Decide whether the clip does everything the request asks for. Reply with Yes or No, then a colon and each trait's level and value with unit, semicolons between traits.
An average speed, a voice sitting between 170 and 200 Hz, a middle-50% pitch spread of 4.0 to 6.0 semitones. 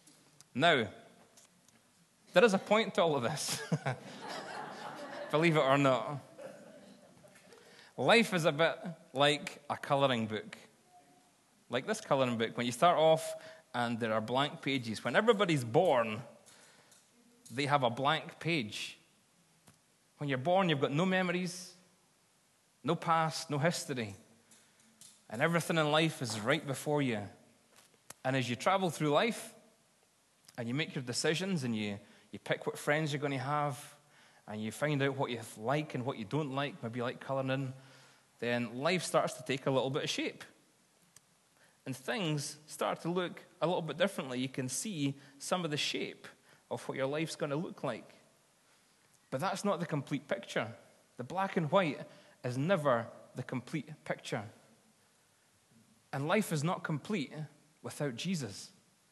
No: average, 155 wpm; medium, 150 Hz; average, 4.7 semitones